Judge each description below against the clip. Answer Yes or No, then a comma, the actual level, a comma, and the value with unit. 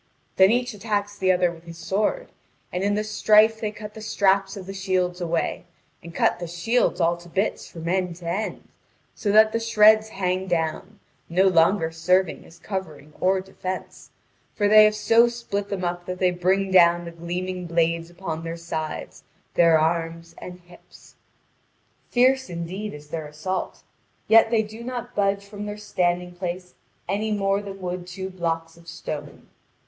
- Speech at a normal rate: Yes, average, 175 wpm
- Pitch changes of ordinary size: Yes, average, 3.4 semitones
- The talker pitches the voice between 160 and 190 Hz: Yes, medium, 185 Hz